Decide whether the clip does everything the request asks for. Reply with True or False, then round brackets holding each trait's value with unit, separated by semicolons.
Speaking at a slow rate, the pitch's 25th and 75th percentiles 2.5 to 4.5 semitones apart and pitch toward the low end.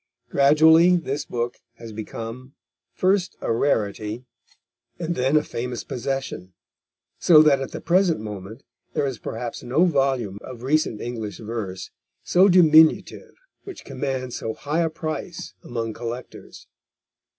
False (130 wpm; 5.4 semitones; 130 Hz)